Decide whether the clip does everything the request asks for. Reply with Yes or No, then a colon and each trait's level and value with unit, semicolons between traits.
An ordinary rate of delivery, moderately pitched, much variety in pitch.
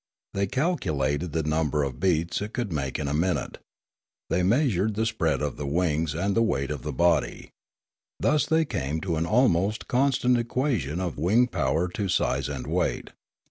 No: average, 180 wpm; very low, 90 Hz; wide, 6.8 semitones